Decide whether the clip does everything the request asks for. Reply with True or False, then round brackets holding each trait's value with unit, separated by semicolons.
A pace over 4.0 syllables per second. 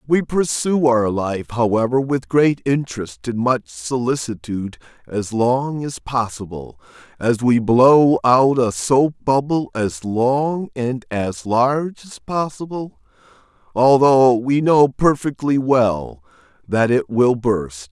False (3.6 syllables/s)